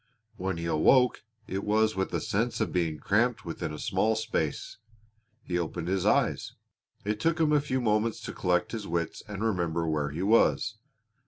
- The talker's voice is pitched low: Yes, low, 100 Hz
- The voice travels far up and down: No, average, 4.8 semitones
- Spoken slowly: No, average, 180 wpm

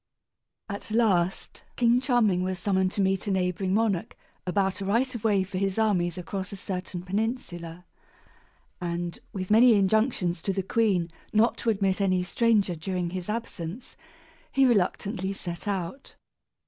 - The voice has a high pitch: Yes, high, 195 Hz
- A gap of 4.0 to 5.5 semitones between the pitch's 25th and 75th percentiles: No, average, 3.2 semitones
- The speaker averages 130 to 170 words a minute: Yes, average, 150 wpm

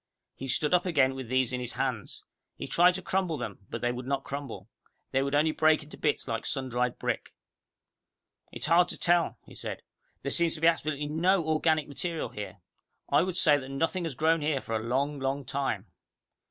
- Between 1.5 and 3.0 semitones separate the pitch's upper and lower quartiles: No, average, 3.9 semitones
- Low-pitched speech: No, medium, 145 Hz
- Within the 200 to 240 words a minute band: Yes, fast, 205 wpm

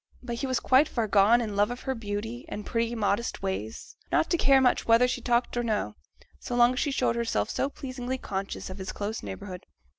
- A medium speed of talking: No, fast, 230 wpm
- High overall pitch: Yes, high, 235 Hz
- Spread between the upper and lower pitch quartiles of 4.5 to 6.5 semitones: No, average, 3.5 semitones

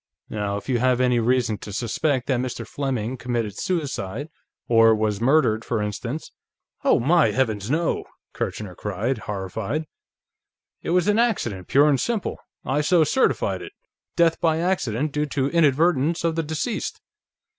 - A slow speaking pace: No, average, 155 wpm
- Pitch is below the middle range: Yes, low, 130 Hz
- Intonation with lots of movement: Yes, wide, 6.0 semitones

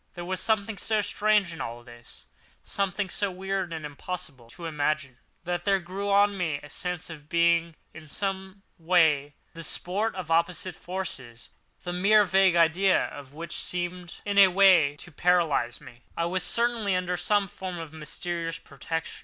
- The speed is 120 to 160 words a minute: No, average, 170 wpm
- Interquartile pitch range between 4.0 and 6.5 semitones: No, average, 3.2 semitones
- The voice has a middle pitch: Yes, medium, 175 Hz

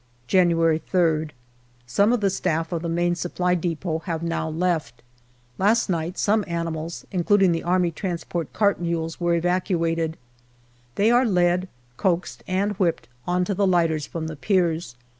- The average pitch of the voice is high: No, medium, 175 Hz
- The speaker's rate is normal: Yes, average, 150 wpm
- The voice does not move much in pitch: Yes, narrow, 2.1 semitones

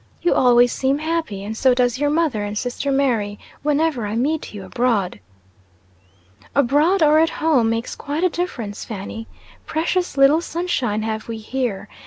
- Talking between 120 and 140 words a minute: No, average, 160 wpm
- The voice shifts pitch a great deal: Yes, wide, 5.9 semitones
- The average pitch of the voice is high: Yes, very high, 255 Hz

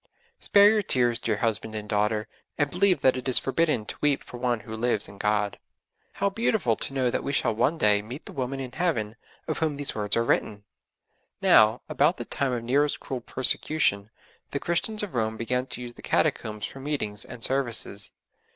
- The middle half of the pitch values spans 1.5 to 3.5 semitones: No, average, 5.0 semitones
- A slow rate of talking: No, average, 200 wpm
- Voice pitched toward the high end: No, low, 125 Hz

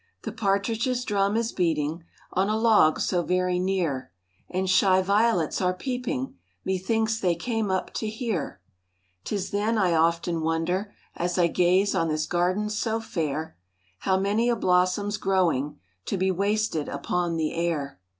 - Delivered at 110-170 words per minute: Yes, average, 155 wpm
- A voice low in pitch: No, medium, 185 Hz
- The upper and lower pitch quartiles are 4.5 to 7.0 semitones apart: No, average, 3.8 semitones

